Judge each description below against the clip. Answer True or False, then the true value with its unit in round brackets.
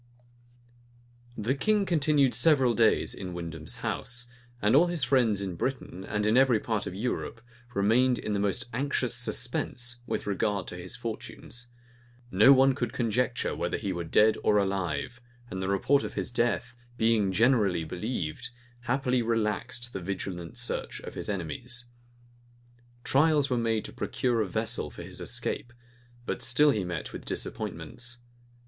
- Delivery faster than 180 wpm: False (155 wpm)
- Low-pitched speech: True (115 Hz)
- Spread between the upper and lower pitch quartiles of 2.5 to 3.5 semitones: False (4.2 semitones)